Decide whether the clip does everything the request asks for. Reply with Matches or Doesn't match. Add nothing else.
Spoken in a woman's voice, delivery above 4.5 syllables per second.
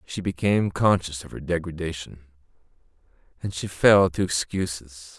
Doesn't match